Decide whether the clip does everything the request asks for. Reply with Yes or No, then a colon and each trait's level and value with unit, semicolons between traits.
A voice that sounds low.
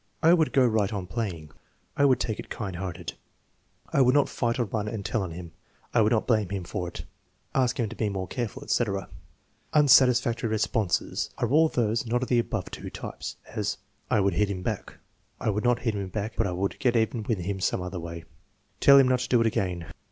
Yes: low, 110 Hz